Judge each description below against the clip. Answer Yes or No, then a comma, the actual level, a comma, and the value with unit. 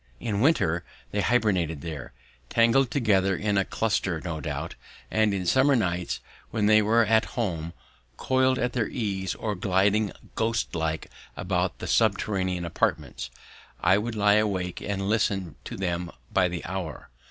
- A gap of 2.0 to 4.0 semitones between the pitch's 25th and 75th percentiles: Yes, average, 3.7 semitones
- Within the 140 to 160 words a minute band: Yes, average, 155 wpm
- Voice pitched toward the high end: No, low, 100 Hz